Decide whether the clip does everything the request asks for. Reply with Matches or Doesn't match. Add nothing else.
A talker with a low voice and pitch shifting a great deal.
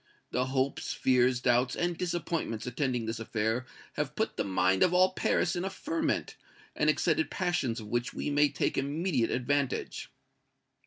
Matches